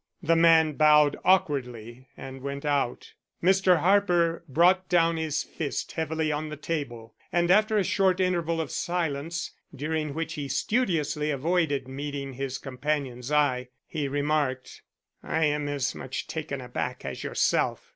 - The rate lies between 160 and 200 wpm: No, average, 145 wpm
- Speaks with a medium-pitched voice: Yes, medium, 150 Hz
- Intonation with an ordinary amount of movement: Yes, average, 3.3 semitones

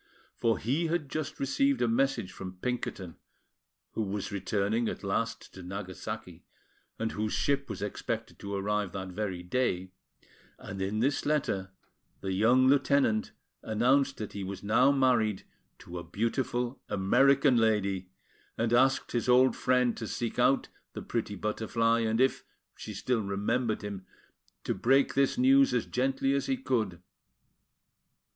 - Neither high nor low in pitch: No, low, 115 Hz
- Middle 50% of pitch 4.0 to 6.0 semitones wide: Yes, average, 4.7 semitones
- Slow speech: No, average, 150 wpm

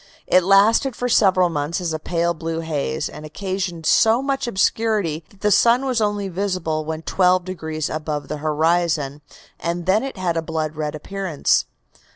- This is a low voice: No, medium, 175 Hz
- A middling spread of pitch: Yes, average, 4.0 semitones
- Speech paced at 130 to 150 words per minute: No, average, 175 wpm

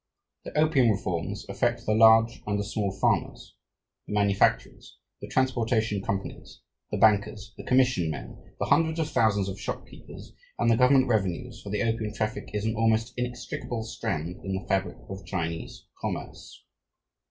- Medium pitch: No, low, 110 Hz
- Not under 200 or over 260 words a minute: No, average, 155 wpm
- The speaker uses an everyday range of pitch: Yes, average, 3.1 semitones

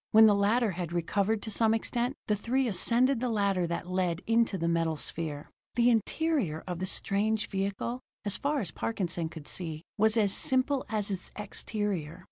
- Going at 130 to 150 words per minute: No, average, 180 wpm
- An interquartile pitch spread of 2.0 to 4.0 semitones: No, average, 4.5 semitones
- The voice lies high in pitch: Yes, high, 205 Hz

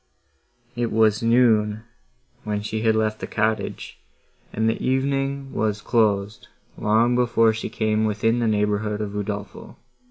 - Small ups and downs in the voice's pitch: Yes, narrow, 1.6 semitones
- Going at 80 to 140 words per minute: Yes, slow, 135 wpm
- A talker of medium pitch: No, low, 110 Hz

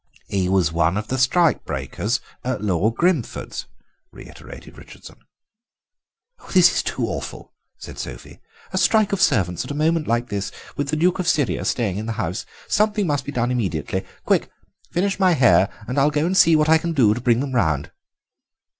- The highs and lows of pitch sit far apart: Yes, wide, 7.9 semitones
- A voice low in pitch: Yes, low, 130 Hz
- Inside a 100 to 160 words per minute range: No, average, 185 wpm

